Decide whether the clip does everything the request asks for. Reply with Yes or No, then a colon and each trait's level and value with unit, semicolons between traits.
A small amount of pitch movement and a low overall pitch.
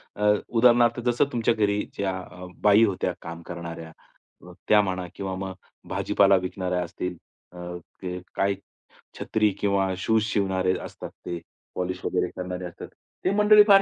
No: average, 3.0 semitones; very low, 95 Hz